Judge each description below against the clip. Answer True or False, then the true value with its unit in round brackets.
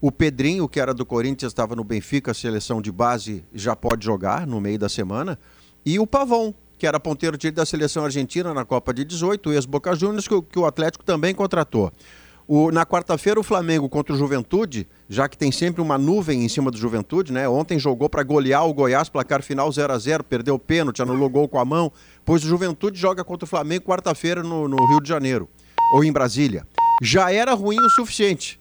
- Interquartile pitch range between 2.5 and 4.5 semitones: False (5.1 semitones)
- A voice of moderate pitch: True (150 Hz)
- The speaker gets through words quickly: True (210 wpm)